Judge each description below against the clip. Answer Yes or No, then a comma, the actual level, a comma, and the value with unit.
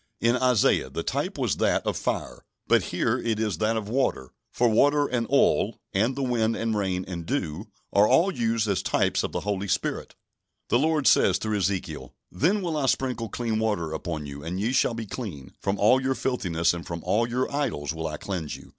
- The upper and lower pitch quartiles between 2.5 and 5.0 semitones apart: No, wide, 5.5 semitones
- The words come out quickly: Yes, fast, 210 wpm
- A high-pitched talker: No, low, 110 Hz